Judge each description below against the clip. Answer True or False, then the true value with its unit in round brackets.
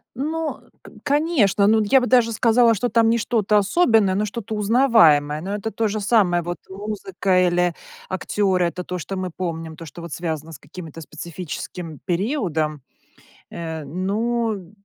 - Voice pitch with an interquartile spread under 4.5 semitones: False (4.8 semitones)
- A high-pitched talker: True (195 Hz)